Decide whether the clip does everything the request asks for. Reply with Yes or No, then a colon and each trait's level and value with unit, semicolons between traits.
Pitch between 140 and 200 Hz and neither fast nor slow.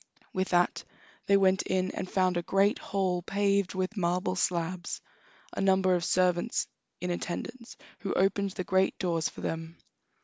Yes: medium, 185 Hz; average, 160 wpm